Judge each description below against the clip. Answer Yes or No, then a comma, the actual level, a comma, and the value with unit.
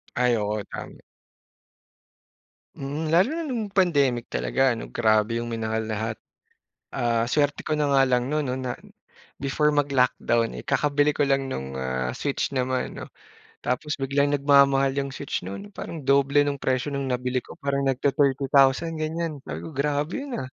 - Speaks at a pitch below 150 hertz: Yes, low, 135 Hz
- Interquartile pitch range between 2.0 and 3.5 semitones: Yes, average, 3.2 semitones